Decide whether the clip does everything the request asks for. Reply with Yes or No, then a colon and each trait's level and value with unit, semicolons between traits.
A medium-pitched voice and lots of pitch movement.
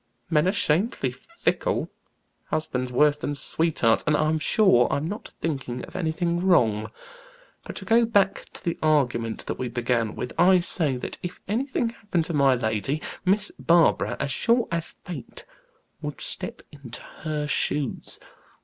Yes: medium, 155 Hz; wide, 6.1 semitones